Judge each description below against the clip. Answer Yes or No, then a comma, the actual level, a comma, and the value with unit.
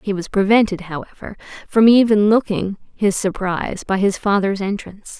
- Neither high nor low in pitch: No, high, 200 Hz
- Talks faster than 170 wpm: No, average, 150 wpm